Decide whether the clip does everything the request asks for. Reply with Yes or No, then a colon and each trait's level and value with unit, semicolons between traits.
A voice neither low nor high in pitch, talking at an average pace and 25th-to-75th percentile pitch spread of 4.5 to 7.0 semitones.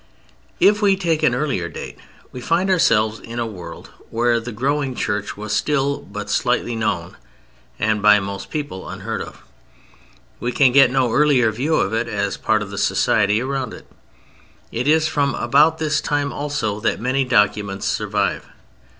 No: low, 125 Hz; average, 165 wpm; wide, 5.5 semitones